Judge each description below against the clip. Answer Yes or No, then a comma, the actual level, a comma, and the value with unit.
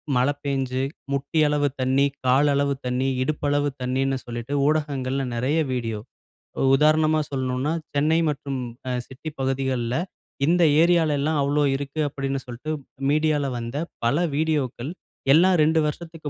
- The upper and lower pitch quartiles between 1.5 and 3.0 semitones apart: Yes, average, 2.7 semitones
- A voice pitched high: No, medium, 140 Hz